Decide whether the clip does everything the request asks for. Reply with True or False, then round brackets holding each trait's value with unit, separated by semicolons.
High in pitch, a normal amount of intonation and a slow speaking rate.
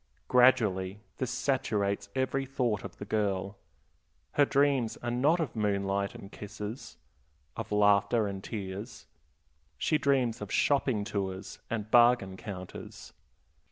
False (105 Hz; 4.1 semitones; 120 wpm)